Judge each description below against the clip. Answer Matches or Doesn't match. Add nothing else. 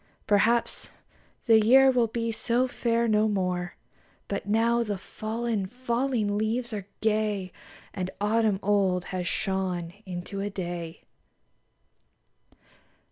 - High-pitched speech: Matches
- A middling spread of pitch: Matches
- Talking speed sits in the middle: Doesn't match